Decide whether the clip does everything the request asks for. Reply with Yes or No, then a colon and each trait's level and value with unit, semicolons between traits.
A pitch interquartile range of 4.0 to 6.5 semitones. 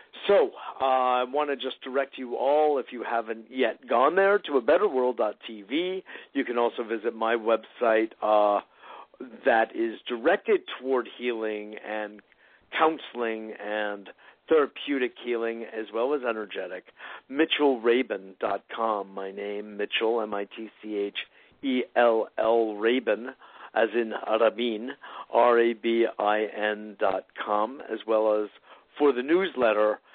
No: average, 3.5 semitones